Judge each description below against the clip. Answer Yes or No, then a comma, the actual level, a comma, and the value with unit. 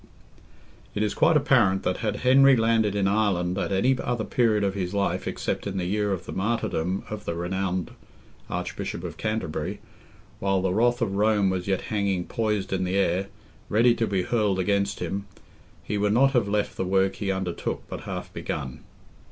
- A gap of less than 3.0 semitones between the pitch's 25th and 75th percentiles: Yes, narrow, 2.6 semitones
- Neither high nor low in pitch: No, low, 100 Hz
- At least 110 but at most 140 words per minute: No, average, 185 wpm